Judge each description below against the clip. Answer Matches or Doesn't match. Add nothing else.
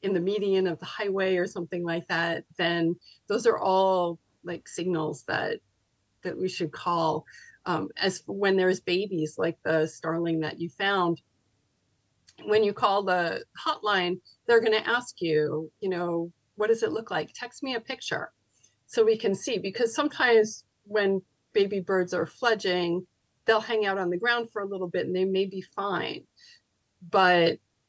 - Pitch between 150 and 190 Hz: Matches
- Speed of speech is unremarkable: Matches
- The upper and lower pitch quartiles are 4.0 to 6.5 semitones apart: Doesn't match